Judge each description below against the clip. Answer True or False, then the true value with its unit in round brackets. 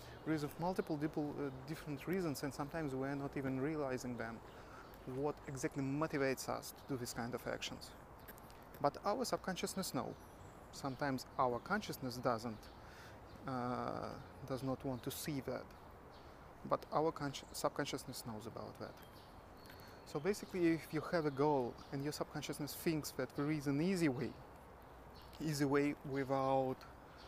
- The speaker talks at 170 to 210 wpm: False (145 wpm)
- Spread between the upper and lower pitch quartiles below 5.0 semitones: True (3.4 semitones)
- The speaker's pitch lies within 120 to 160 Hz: True (140 Hz)